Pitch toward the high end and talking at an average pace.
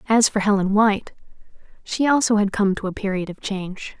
Yes: high, 205 Hz; average, 195 wpm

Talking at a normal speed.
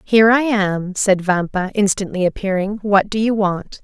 Yes: average, 170 wpm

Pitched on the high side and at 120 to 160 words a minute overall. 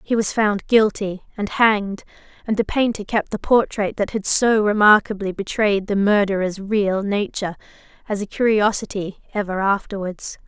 Yes: high, 205 Hz; average, 150 wpm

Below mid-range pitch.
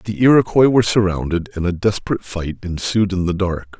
Yes: very low, 95 Hz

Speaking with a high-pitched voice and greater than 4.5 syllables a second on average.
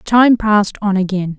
No: high, 205 Hz; 4.4 syllables/s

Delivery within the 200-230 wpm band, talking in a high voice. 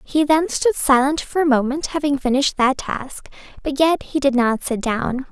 Yes: fast, 205 wpm; very high, 275 Hz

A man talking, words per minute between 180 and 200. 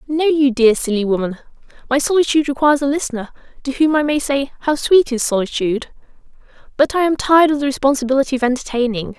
No: female; average, 185 wpm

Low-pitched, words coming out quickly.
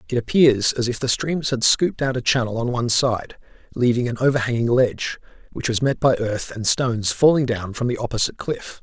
Yes: low, 120 Hz; fast, 210 wpm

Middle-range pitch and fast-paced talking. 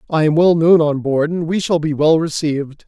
Yes: medium, 160 Hz; fast, 250 wpm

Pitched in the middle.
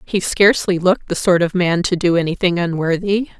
Yes: medium, 180 Hz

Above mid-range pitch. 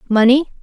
Yes: very high, 250 Hz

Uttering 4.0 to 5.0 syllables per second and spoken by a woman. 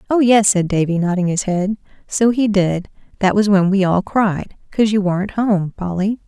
Yes: 4.9 syllables/s; female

